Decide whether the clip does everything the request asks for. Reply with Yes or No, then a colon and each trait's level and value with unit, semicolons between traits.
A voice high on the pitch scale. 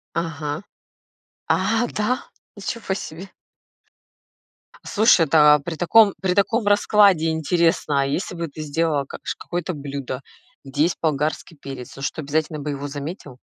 No: medium, 160 Hz